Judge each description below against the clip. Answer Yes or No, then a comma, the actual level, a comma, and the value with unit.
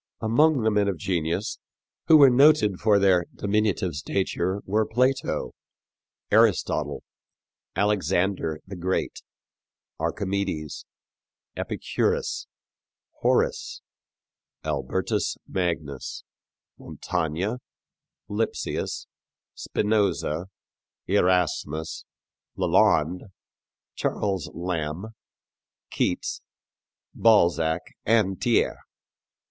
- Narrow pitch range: No, average, 4.0 semitones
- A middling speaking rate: No, slow, 70 wpm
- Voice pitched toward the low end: Yes, very low, 95 Hz